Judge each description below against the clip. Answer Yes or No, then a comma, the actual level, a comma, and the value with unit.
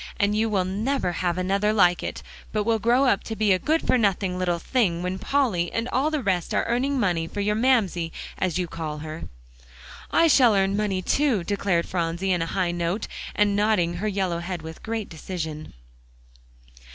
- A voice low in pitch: No, high, 195 Hz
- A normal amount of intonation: Yes, average, 4.1 semitones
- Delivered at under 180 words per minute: No, average, 195 wpm